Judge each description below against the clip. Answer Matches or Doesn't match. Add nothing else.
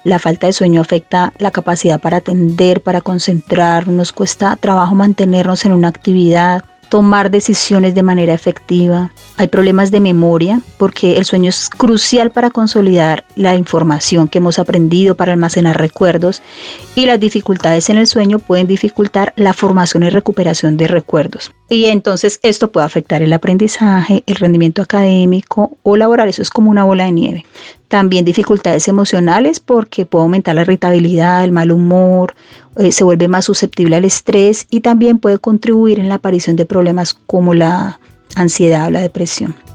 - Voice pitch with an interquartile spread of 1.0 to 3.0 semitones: Matches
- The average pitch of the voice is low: Doesn't match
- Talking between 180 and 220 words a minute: Doesn't match